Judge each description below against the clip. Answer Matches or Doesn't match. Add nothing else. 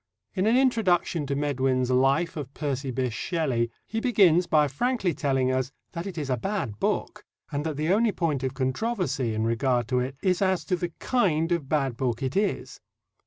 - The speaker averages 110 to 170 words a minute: Doesn't match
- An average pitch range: Doesn't match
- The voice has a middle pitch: Matches